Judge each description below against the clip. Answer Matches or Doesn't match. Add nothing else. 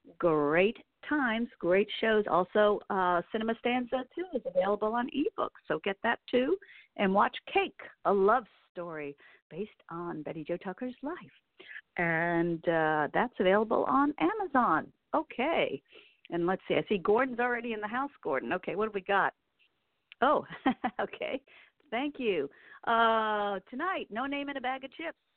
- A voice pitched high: Matches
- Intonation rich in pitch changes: Matches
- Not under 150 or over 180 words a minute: Matches